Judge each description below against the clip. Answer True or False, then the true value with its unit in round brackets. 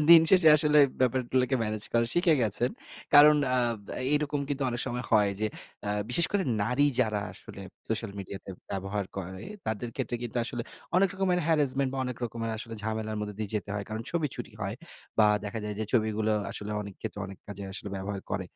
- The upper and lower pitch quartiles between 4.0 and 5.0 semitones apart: True (4.7 semitones)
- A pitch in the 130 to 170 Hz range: False (115 Hz)